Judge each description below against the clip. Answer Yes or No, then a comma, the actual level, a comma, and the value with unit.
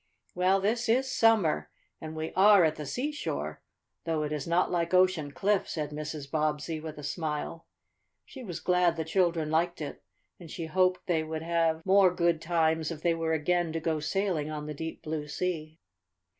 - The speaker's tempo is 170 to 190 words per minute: Yes, average, 185 wpm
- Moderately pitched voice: Yes, medium, 165 Hz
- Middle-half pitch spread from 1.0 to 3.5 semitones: Yes, average, 2.8 semitones